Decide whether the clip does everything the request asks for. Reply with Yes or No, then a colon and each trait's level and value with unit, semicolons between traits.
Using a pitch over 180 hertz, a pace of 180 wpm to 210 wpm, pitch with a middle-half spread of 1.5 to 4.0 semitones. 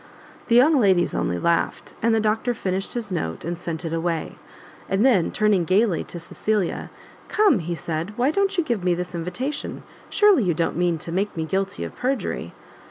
No: high, 190 Hz; average, 190 wpm; wide, 5.6 semitones